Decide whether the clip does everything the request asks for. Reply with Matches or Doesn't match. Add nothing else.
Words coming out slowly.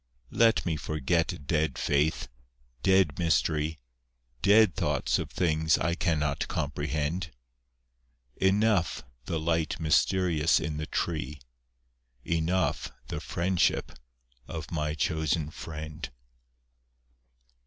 Matches